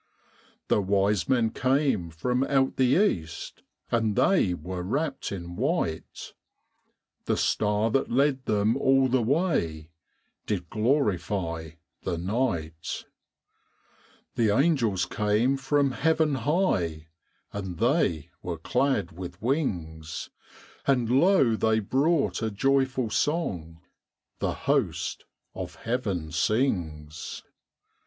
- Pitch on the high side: No, low, 110 Hz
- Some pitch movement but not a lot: No, wide, 7.3 semitones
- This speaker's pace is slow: Yes, slow, 105 wpm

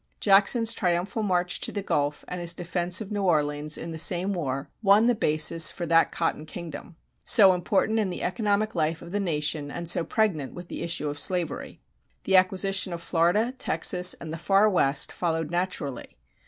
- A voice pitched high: No, medium, 175 Hz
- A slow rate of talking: No, average, 185 wpm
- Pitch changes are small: No, average, 3.5 semitones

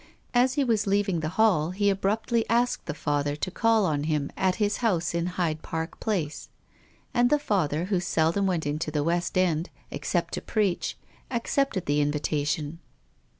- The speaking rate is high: No, average, 170 wpm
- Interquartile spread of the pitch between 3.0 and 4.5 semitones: No, wide, 5.6 semitones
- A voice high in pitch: No, medium, 180 Hz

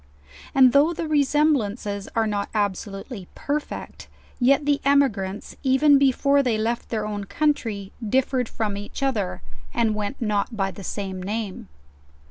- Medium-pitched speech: No, high, 225 Hz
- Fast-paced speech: No, average, 145 wpm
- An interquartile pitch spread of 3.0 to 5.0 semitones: No, wide, 5.4 semitones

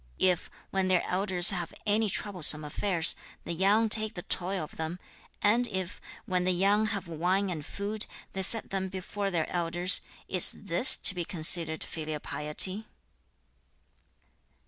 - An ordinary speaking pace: Yes, average, 150 wpm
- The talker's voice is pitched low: No, medium, 185 Hz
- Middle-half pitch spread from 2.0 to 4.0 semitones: Yes, average, 2.9 semitones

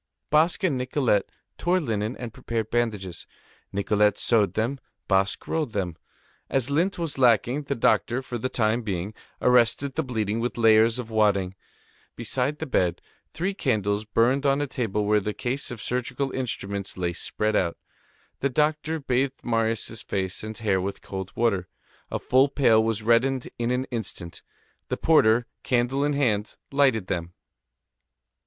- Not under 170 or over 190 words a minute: No, average, 160 wpm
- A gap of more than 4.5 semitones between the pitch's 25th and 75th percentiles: No, average, 4.2 semitones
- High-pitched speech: No, low, 115 Hz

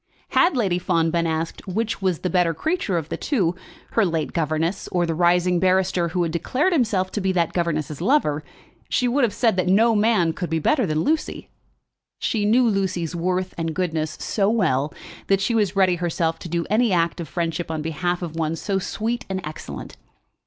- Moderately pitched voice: Yes, medium, 180 Hz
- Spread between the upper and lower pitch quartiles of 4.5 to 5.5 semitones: No, average, 3.8 semitones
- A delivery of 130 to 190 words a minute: No, average, 200 wpm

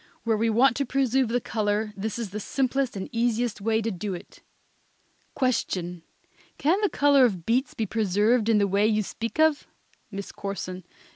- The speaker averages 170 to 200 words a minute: Yes, average, 175 wpm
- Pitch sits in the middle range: No, high, 225 Hz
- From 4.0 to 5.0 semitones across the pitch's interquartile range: No, average, 3.6 semitones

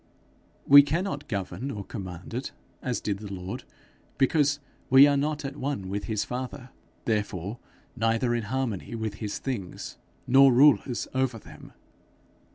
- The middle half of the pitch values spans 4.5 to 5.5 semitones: Yes, average, 4.9 semitones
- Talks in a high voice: No, low, 125 Hz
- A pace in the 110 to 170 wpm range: Yes, average, 150 wpm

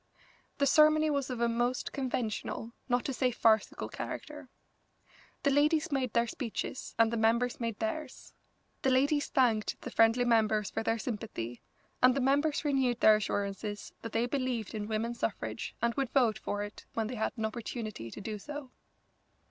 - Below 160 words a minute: No, average, 170 wpm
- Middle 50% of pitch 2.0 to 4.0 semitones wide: Yes, average, 3.6 semitones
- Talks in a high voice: Yes, high, 235 Hz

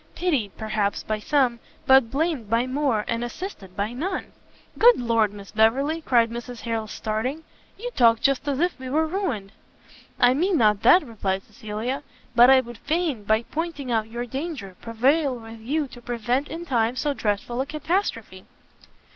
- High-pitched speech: Yes, high, 245 Hz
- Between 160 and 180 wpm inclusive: Yes, average, 170 wpm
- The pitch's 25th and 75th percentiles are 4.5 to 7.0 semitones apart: Yes, average, 4.9 semitones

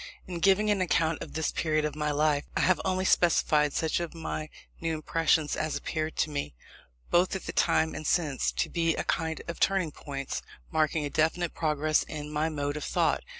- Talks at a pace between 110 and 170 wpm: No, average, 200 wpm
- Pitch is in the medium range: Yes, medium, 155 Hz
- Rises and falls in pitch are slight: Yes, narrow, 1.9 semitones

